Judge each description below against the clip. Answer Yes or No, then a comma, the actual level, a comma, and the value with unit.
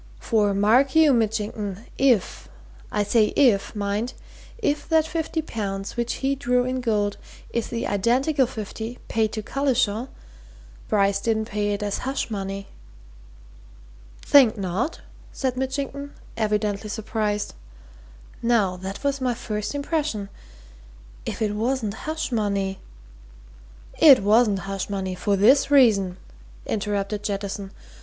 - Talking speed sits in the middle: No, slow, 125 wpm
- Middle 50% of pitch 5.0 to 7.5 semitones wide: No, average, 4.3 semitones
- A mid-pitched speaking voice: No, high, 220 Hz